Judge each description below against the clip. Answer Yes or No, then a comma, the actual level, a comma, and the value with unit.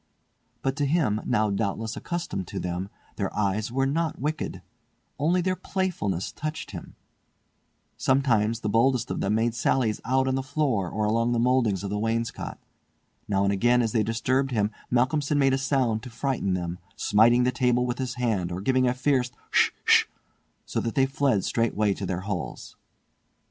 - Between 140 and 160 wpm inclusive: No, average, 180 wpm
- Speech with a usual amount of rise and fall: Yes, average, 4.2 semitones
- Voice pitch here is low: Yes, low, 120 Hz